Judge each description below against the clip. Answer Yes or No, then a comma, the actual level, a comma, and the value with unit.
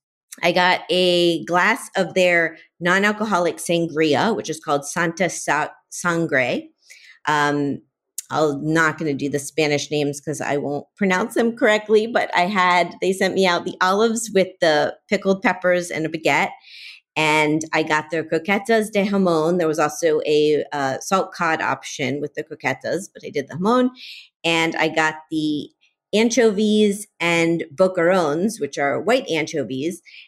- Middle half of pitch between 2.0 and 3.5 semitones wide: No, average, 4.1 semitones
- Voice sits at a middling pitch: Yes, medium, 170 Hz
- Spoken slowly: No, average, 155 wpm